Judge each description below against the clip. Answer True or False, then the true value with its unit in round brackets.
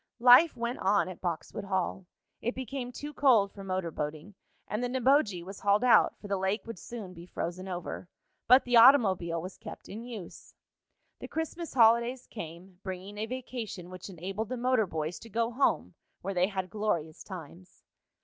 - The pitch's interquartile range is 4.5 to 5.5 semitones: True (4.9 semitones)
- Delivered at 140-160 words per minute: False (180 wpm)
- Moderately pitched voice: False (205 Hz)